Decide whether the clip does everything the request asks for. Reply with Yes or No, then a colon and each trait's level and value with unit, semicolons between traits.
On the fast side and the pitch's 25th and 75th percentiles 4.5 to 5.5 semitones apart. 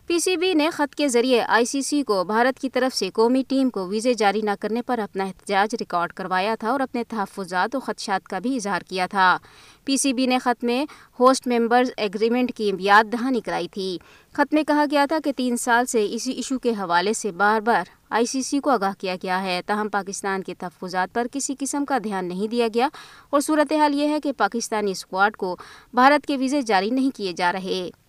Yes: fast, 220 wpm; average, 5.2 semitones